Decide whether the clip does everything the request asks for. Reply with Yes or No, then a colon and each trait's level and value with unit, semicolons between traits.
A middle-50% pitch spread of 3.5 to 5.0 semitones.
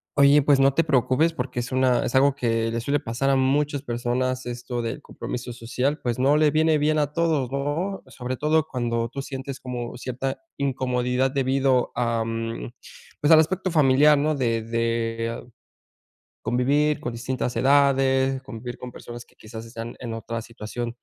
No: average, 3.0 semitones